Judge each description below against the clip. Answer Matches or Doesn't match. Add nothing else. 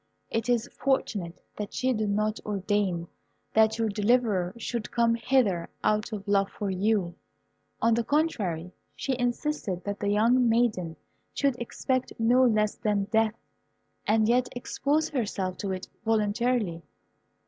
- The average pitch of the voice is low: Doesn't match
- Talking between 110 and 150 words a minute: Matches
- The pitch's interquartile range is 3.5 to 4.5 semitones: Doesn't match